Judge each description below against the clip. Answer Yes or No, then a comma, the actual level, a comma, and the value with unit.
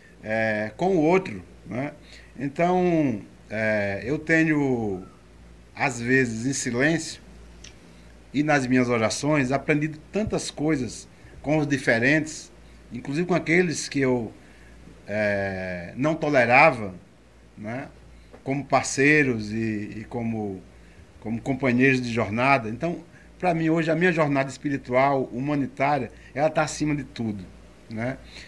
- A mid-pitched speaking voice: No, low, 130 Hz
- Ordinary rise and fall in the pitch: No, wide, 7.1 semitones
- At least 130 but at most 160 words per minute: No, slow, 120 wpm